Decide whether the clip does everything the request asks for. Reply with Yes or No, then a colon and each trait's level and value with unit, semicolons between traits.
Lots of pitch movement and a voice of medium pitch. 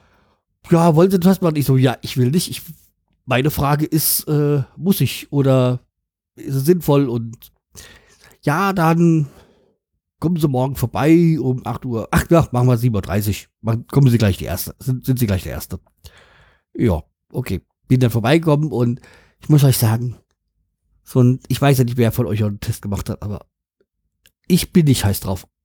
No: wide, 6.0 semitones; low, 125 Hz